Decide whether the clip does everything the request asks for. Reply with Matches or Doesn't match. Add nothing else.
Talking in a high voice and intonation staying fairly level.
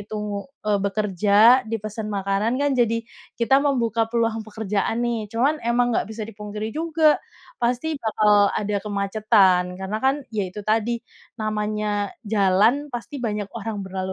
Matches